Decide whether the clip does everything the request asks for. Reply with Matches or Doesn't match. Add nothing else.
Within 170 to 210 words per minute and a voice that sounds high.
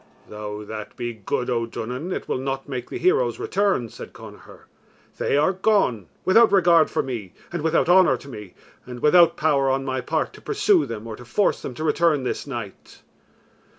Doesn't match